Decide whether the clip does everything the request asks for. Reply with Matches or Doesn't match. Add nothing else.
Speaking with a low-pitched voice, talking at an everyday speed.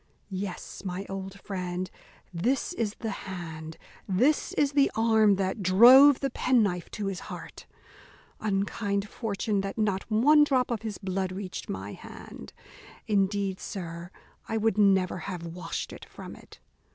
Doesn't match